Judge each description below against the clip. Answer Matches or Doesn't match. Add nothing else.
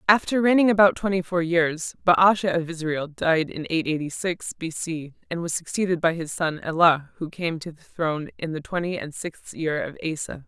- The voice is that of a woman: Matches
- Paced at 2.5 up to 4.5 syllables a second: Doesn't match